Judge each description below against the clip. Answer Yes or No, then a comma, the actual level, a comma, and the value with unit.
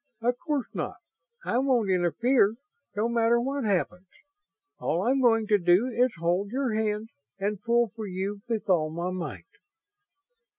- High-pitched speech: Yes, high, 215 Hz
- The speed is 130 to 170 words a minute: Yes, average, 155 wpm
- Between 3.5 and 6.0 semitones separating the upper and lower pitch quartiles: Yes, average, 4.1 semitones